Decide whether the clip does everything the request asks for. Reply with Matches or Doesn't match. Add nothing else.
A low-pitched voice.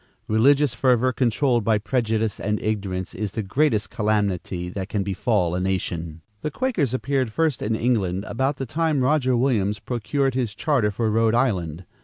Matches